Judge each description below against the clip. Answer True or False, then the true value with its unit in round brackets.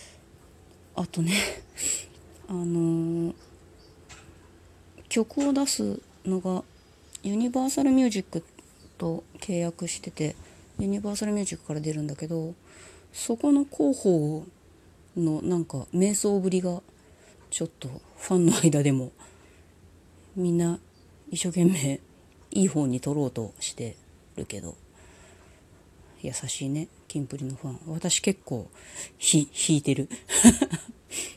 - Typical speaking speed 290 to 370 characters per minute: False (220 characters per minute)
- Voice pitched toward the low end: False (155 Hz)